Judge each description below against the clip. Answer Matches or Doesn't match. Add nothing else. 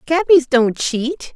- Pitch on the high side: Matches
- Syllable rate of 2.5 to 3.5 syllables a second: Matches